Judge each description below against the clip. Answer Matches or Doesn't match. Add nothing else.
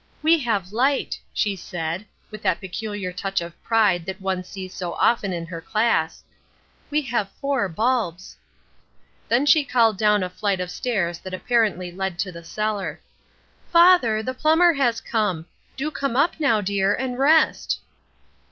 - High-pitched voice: Matches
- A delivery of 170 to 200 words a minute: Doesn't match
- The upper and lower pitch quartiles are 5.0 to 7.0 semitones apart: Matches